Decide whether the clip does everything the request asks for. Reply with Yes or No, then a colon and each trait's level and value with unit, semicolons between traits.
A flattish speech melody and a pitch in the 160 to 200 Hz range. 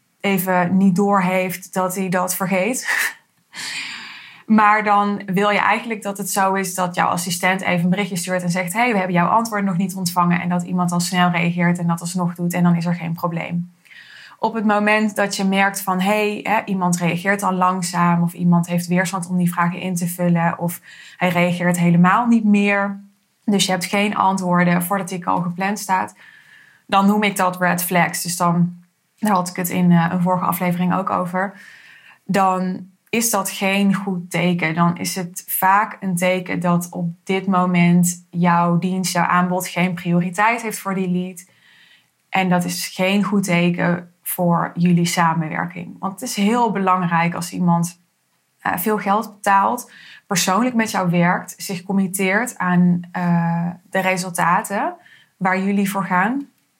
Yes: narrow, 2.1 semitones; medium, 185 Hz